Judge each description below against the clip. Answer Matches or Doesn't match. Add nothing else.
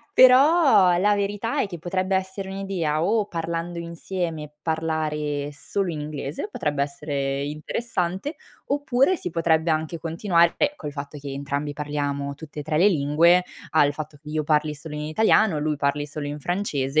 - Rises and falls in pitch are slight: Doesn't match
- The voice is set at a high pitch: Doesn't match